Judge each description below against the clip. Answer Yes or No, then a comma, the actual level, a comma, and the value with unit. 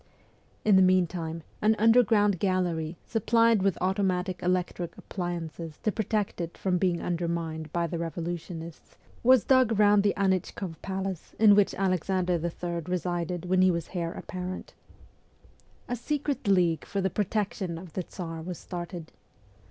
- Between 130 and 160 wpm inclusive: Yes, average, 145 wpm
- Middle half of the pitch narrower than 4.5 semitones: Yes, average, 2.8 semitones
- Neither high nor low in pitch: Yes, medium, 180 Hz